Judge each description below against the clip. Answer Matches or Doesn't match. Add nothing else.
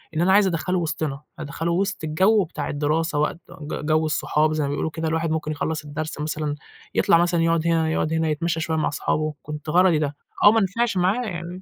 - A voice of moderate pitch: Matches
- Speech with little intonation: Matches